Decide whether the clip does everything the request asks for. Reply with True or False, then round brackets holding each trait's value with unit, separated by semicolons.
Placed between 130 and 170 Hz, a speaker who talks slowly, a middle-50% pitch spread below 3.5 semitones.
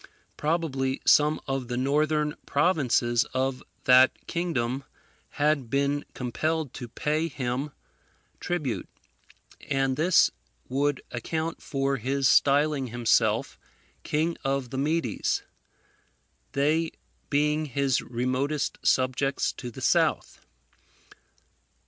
True (140 Hz; 100 wpm; 2.9 semitones)